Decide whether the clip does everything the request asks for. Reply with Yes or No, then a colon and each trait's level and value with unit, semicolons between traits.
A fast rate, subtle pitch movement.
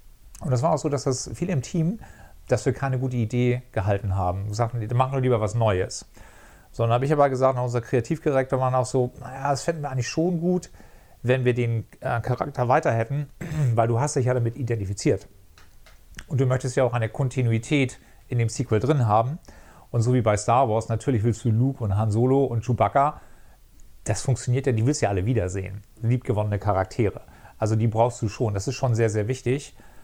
No: fast, 205 wpm; average, 3.2 semitones